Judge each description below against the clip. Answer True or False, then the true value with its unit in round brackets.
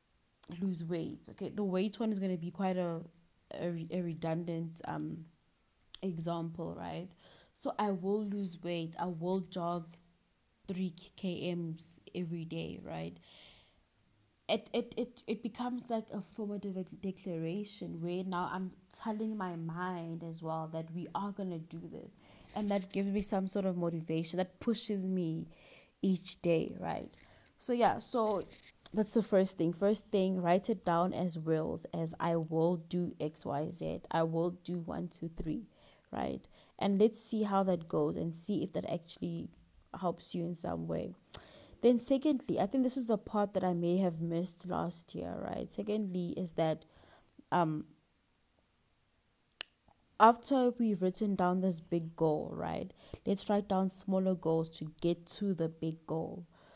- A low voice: False (180 Hz)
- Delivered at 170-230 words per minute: False (160 wpm)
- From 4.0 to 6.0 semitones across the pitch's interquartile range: False (3.3 semitones)